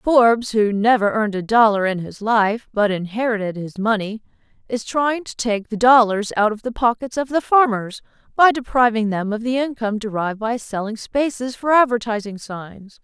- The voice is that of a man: No, female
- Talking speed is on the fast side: No, average, 180 wpm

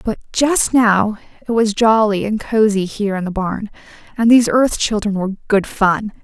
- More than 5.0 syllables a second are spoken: No, 4.8 syllables/s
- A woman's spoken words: Yes, female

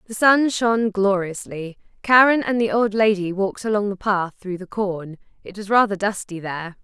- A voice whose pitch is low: No, high, 200 Hz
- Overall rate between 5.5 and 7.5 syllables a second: No, 5.1 syllables/s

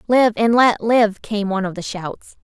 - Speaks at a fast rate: Yes, fast, 215 wpm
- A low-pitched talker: No, high, 215 Hz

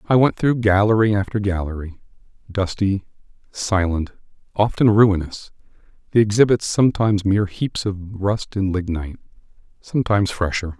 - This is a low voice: Yes, low, 100 Hz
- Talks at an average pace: No, slow, 115 wpm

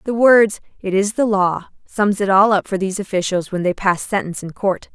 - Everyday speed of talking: No, fast, 230 wpm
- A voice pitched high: Yes, high, 195 Hz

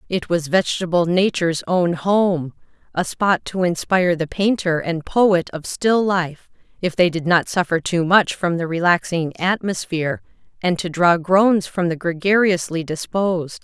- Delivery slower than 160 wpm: Yes, average, 150 wpm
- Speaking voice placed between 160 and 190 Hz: Yes, medium, 175 Hz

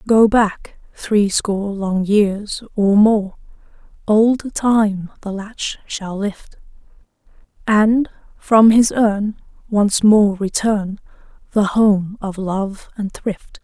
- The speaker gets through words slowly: Yes, slow, 115 wpm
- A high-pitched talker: Yes, high, 205 Hz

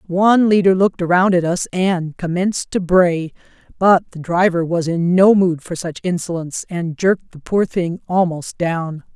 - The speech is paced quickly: No, average, 175 wpm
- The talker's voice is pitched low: No, medium, 180 Hz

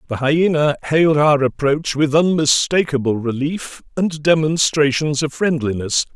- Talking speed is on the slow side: Yes, slow, 115 wpm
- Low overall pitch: No, medium, 150 Hz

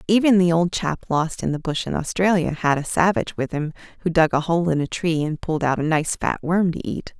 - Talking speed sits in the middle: No, fast, 260 wpm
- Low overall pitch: No, medium, 165 Hz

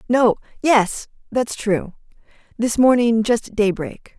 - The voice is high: Yes, high, 225 Hz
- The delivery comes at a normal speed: No, slow, 85 wpm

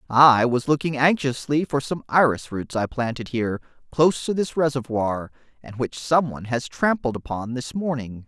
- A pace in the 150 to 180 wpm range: Yes, average, 175 wpm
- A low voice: Yes, low, 130 Hz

